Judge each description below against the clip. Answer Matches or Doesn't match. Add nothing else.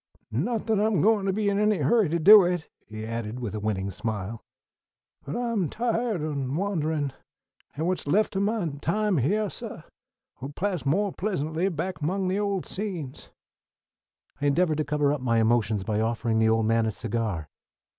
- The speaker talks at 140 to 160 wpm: Doesn't match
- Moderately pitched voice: Matches